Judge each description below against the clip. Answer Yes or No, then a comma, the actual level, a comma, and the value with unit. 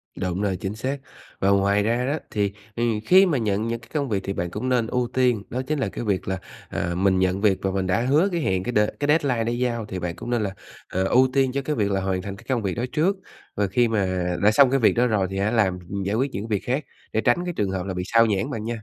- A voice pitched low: Yes, low, 110 Hz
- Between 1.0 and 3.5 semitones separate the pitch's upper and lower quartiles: No, average, 4.5 semitones